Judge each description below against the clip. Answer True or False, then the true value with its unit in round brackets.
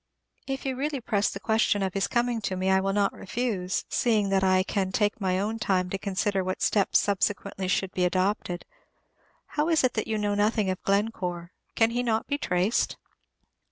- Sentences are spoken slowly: False (195 wpm)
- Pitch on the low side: False (200 Hz)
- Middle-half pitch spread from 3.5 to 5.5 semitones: False (3.0 semitones)